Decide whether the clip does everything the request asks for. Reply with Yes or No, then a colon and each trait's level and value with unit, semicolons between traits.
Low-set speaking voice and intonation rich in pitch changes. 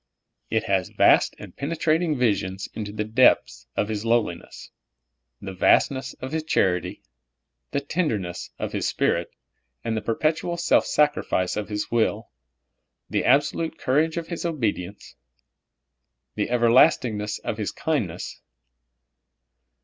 Yes: low, 115 Hz; wide, 6.4 semitones